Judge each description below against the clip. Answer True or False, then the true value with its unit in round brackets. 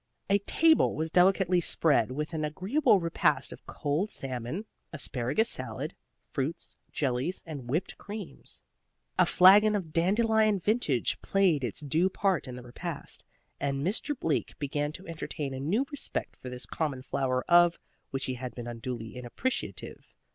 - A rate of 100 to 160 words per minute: True (150 wpm)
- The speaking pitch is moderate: True (160 Hz)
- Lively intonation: True (6.6 semitones)